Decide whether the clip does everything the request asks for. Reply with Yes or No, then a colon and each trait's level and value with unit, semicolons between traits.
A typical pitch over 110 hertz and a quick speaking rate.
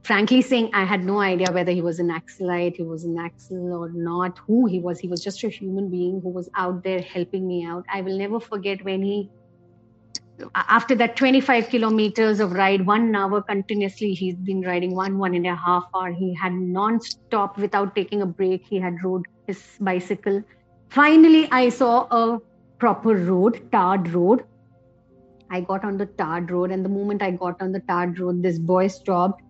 Yes: high, 190 Hz; fast, 195 wpm